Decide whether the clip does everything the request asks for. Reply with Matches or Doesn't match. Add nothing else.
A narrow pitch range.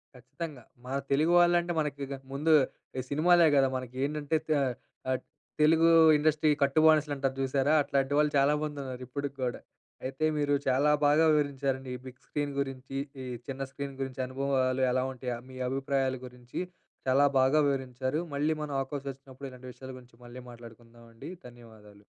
Matches